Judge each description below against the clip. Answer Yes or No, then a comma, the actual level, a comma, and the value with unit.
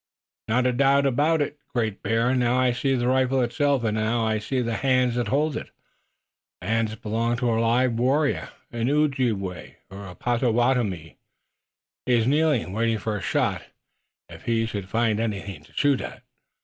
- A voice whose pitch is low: Yes, low, 120 Hz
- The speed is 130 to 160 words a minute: No, average, 175 wpm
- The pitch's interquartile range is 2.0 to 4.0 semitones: Yes, average, 2.7 semitones